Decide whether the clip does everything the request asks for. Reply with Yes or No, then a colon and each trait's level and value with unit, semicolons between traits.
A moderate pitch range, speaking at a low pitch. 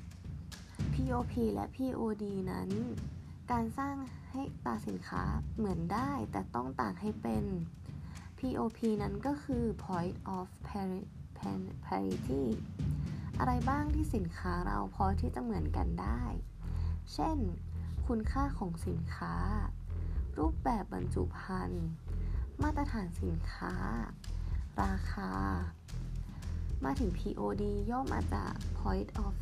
Yes: average, 4.4 semitones; very low, 90 Hz